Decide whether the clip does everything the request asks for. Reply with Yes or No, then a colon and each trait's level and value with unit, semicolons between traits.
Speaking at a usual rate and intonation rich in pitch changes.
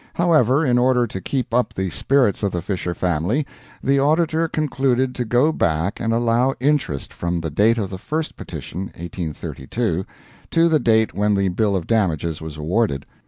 Yes: average, 175 wpm; wide, 7.0 semitones